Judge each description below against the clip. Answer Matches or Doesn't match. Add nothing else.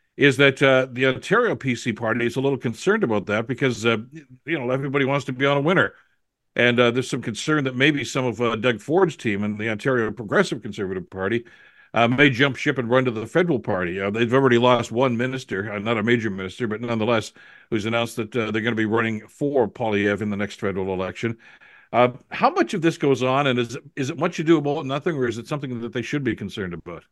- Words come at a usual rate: Doesn't match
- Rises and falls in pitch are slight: Doesn't match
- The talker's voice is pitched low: Matches